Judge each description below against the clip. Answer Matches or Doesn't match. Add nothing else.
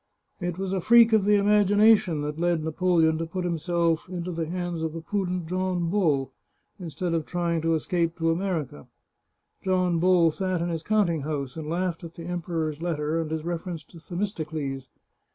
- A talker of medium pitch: Matches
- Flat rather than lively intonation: Matches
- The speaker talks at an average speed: Matches